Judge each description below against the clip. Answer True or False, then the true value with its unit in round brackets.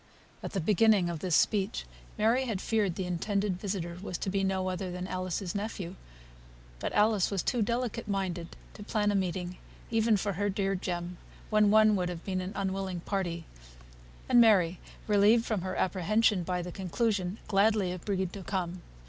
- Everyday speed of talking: True (175 wpm)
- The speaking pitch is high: True (195 Hz)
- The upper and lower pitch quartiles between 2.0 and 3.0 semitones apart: True (2.7 semitones)